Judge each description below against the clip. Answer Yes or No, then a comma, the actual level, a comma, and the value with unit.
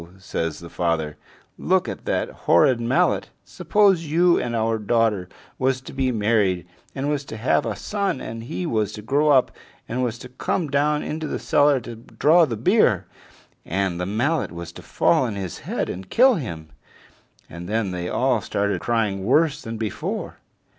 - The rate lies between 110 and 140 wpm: No, average, 180 wpm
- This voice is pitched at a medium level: No, low, 115 Hz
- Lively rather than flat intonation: Yes, wide, 6.7 semitones